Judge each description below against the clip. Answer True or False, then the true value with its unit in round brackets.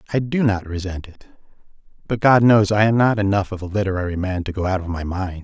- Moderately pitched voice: False (100 Hz)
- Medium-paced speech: False (245 wpm)